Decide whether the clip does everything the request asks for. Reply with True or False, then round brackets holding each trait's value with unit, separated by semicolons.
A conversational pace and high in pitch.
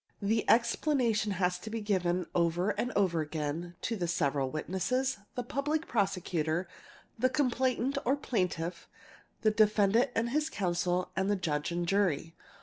True (145 wpm; 195 Hz)